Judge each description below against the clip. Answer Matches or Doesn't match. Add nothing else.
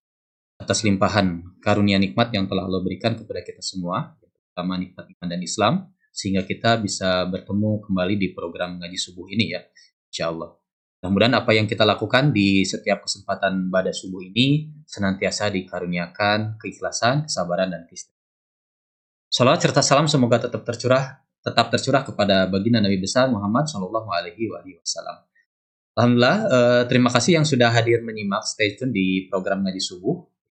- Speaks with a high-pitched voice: Doesn't match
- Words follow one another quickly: Matches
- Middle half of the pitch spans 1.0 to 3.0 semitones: Doesn't match